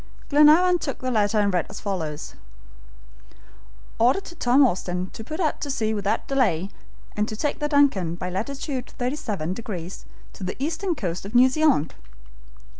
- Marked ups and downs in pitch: Yes, wide, 7.2 semitones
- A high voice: Yes, high, 230 Hz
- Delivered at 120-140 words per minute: No, average, 165 wpm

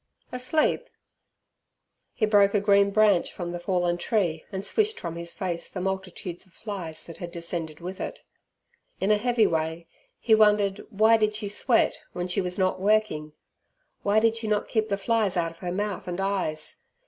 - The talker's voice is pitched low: No, high, 195 Hz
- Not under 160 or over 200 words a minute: Yes, average, 185 wpm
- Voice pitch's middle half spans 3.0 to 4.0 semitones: Yes, average, 3.5 semitones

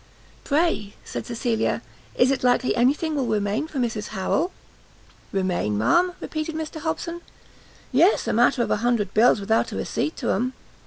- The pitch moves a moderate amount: No, wide, 6.4 semitones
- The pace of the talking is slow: No, average, 165 wpm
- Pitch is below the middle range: No, high, 245 Hz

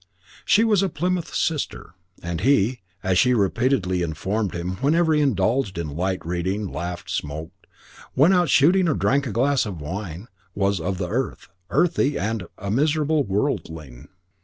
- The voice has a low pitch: Yes, low, 105 Hz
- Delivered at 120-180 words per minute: Yes, average, 160 wpm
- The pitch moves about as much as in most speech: No, wide, 8.0 semitones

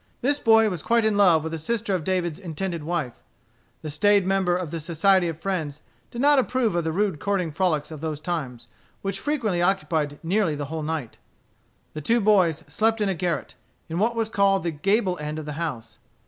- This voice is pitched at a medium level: Yes, medium, 175 Hz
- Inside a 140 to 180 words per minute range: No, fast, 205 wpm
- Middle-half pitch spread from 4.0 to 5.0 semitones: Yes, average, 4.5 semitones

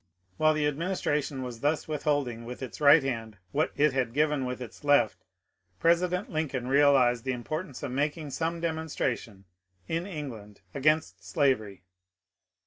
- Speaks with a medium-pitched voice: Yes, medium, 145 Hz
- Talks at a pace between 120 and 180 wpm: Yes, average, 140 wpm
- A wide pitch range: No, average, 3.8 semitones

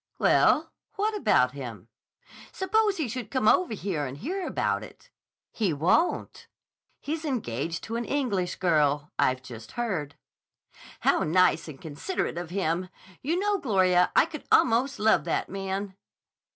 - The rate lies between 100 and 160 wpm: Yes, average, 145 wpm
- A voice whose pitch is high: Yes, high, 195 Hz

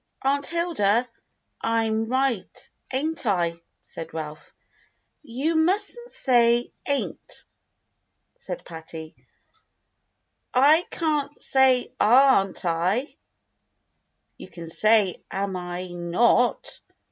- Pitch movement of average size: No, wide, 7.5 semitones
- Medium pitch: No, high, 235 Hz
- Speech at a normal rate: No, slow, 90 wpm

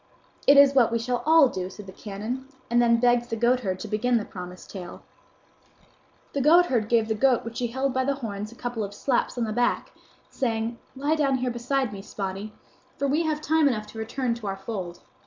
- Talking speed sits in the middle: No, fast, 215 wpm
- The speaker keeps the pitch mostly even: No, average, 3.7 semitones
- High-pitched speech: Yes, high, 235 Hz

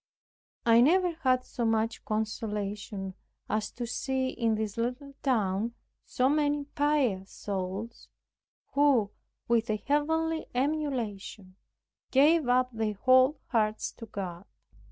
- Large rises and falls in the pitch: No, average, 4.7 semitones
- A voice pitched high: Yes, high, 235 Hz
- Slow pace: Yes, slow, 115 wpm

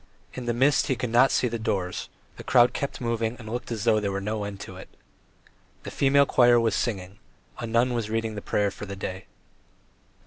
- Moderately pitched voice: No, low, 115 Hz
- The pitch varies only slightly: No, average, 3.0 semitones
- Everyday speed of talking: No, fast, 215 wpm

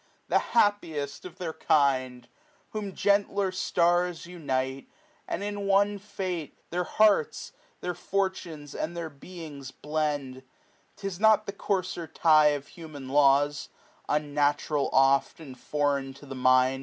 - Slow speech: Yes, slow, 130 wpm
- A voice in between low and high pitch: Yes, medium, 155 Hz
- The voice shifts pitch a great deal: No, average, 4.8 semitones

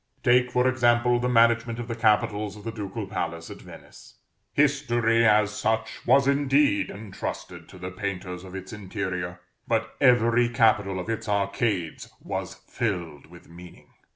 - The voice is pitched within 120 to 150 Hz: No, low, 110 Hz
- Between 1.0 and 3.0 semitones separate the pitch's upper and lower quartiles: No, average, 3.9 semitones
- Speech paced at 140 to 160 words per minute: Yes, average, 155 wpm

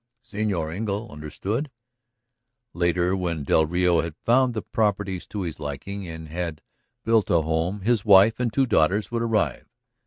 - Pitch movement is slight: No, average, 4.7 semitones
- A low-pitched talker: Yes, very low, 95 Hz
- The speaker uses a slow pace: No, average, 155 wpm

